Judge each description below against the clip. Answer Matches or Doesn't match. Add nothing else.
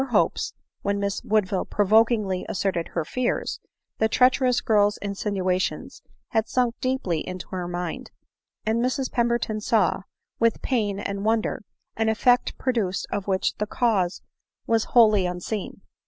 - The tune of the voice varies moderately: Matches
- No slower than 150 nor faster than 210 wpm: Doesn't match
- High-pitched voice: Matches